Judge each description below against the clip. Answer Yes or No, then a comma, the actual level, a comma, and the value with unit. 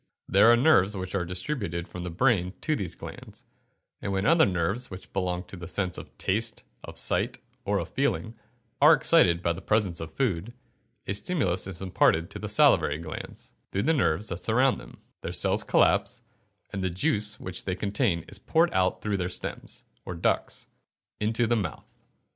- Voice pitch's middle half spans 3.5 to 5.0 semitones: Yes, average, 4.1 semitones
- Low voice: Yes, very low, 95 Hz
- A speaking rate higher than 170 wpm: Yes, average, 185 wpm